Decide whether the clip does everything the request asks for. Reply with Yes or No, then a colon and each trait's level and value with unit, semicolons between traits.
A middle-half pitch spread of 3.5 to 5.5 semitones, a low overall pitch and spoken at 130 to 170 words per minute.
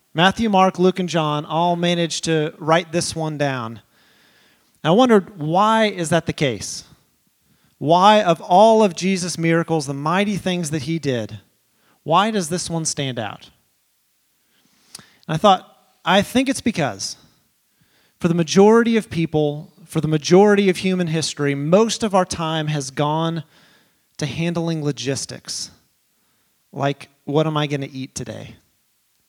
No: average, 4.2 semitones; medium, 165 Hz; average, 150 wpm